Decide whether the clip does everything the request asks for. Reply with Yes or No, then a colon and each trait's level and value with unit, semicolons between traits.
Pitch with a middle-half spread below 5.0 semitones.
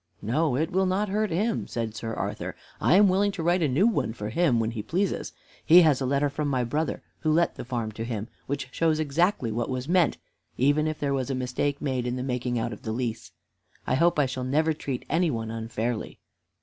No: wide, 5.4 semitones